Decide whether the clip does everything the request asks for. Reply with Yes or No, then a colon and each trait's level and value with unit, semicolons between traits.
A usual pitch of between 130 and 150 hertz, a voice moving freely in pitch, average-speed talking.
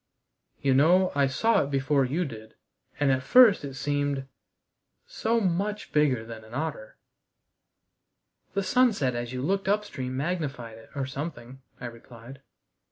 Yes: medium, 140 Hz; wide, 5.7 semitones; average, 145 wpm